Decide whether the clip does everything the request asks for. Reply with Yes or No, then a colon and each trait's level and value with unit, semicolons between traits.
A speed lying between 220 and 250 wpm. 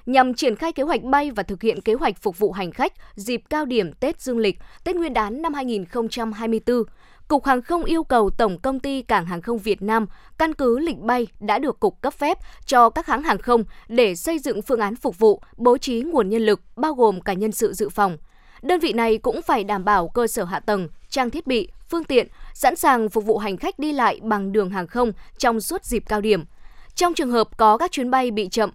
Yes: average, 240 wpm